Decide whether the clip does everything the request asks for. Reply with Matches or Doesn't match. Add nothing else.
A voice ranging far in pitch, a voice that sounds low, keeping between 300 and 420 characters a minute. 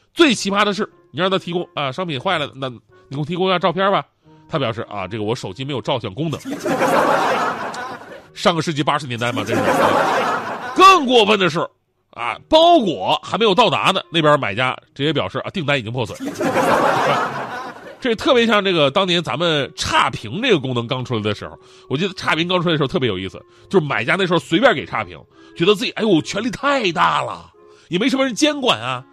Doesn't match